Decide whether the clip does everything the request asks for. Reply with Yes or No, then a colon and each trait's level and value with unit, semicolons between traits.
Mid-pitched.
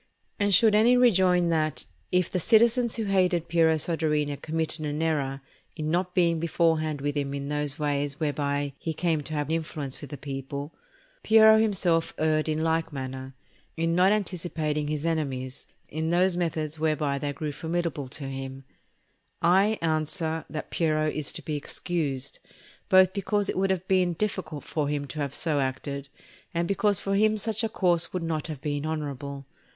Yes: medium, 160 Hz